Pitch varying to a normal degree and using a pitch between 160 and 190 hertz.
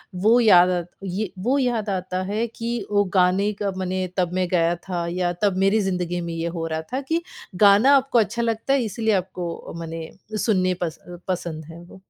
Yes: average, 3.7 semitones; medium, 185 Hz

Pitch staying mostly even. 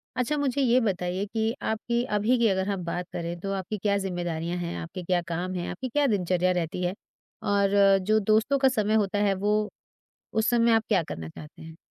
No: average, 3.9 semitones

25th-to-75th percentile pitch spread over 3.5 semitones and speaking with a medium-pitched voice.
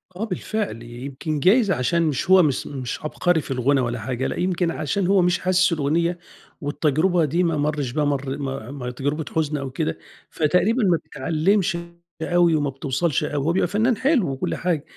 Yes: average, 4.5 semitones; medium, 155 Hz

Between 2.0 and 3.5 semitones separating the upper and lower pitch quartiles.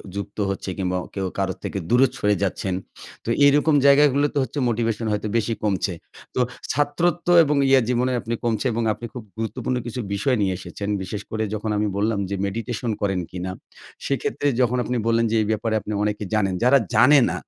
No: average, 4.0 semitones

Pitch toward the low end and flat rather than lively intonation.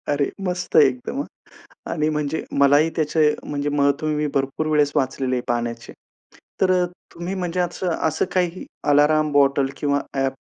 No: medium, 150 Hz; narrow, 2.2 semitones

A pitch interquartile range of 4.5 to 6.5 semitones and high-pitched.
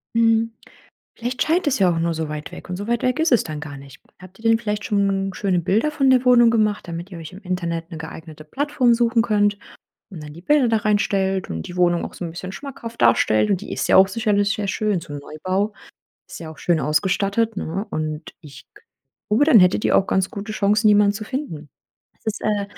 Yes: average, 5.0 semitones; high, 200 Hz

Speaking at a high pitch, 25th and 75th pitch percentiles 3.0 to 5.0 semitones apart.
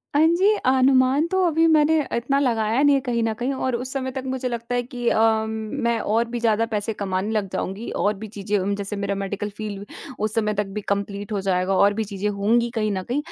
Yes: high, 220 Hz; average, 4.0 semitones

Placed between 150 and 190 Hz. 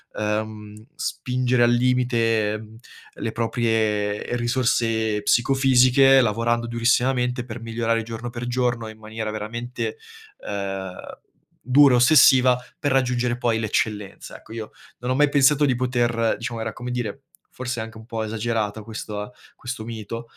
No: low, 115 Hz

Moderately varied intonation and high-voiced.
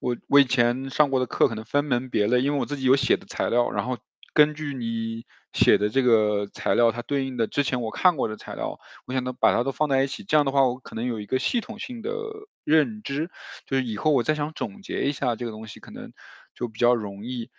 No: average, 3.5 semitones; low, 130 Hz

